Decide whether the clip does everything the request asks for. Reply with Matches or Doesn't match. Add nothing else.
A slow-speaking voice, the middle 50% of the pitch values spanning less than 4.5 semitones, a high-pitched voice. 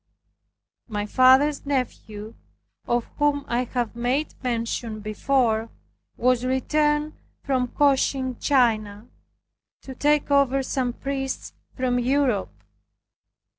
Matches